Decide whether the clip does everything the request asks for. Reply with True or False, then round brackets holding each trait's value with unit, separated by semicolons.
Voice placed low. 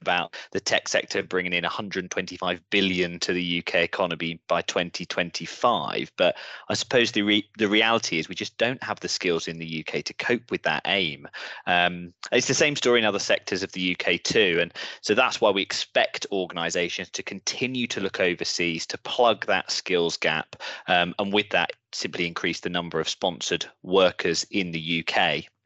True (90 Hz)